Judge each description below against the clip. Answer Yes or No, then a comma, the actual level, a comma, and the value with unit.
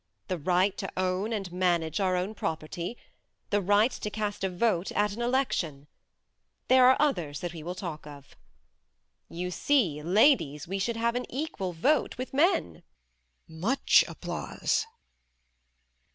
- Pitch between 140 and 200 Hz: Yes, medium, 185 Hz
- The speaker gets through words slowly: No, average, 145 wpm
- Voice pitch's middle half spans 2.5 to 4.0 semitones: No, average, 5.3 semitones